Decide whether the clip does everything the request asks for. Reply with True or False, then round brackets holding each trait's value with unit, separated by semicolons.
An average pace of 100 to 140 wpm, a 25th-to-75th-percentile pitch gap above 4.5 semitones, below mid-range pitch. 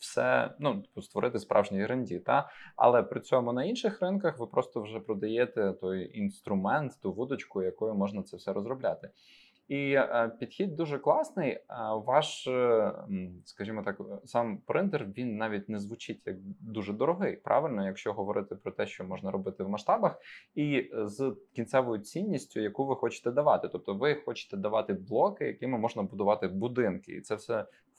False (155 wpm; 5.2 semitones; 120 Hz)